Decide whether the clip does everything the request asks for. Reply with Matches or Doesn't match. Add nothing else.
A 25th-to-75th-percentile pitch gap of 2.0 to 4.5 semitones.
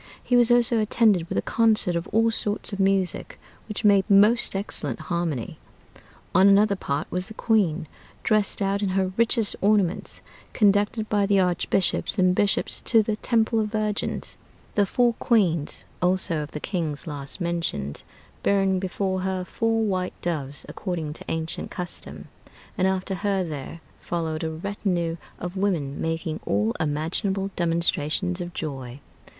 Matches